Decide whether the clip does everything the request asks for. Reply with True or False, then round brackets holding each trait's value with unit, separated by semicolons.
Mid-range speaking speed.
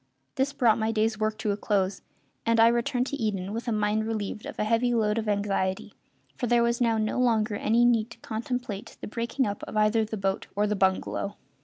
False (220 wpm)